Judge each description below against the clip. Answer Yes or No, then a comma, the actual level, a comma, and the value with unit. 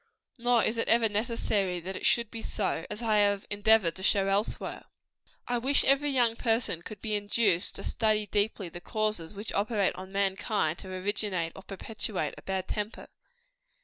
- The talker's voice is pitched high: Yes, high, 205 Hz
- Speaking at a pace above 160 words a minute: Yes, average, 180 wpm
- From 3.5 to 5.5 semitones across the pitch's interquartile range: No, average, 2.7 semitones